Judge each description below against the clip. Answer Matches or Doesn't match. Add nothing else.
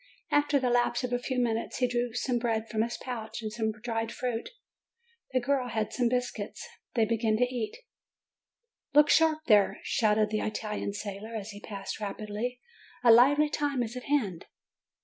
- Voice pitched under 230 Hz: Doesn't match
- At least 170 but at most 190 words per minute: Matches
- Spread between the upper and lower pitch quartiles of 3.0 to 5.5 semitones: Doesn't match